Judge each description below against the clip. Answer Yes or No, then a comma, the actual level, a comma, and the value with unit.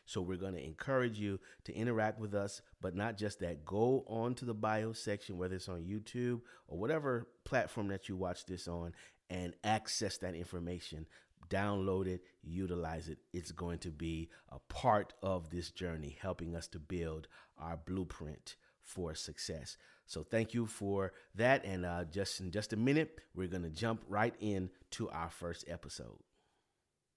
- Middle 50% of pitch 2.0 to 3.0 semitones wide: No, average, 3.6 semitones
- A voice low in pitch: Yes, very low, 95 Hz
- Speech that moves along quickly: No, average, 170 wpm